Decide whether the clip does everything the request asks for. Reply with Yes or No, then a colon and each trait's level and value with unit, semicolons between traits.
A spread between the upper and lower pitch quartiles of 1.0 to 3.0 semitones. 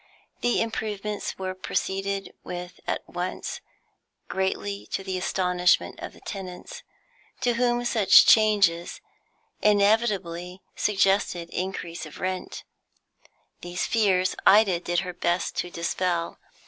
Yes: narrow, 2.6 semitones